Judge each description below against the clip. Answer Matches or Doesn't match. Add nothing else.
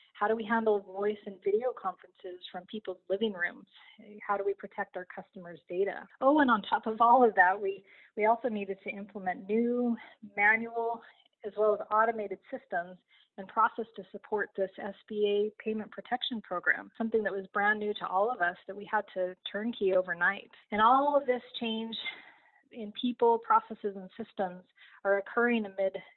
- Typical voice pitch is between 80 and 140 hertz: Doesn't match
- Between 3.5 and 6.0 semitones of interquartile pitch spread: Doesn't match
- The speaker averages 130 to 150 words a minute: Doesn't match